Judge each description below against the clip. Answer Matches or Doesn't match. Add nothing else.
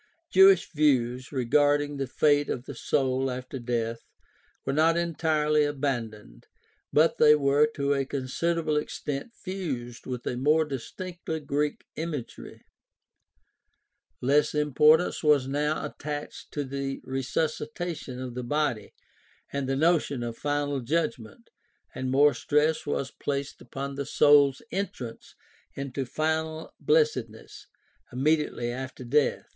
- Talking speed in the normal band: Doesn't match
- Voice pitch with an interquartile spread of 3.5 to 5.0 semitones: Doesn't match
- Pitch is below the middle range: Doesn't match